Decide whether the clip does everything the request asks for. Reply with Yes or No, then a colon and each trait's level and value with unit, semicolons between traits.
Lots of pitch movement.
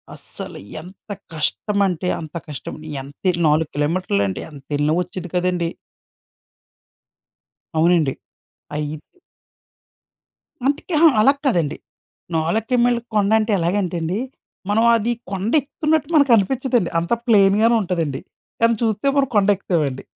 Yes: wide, 5.9 semitones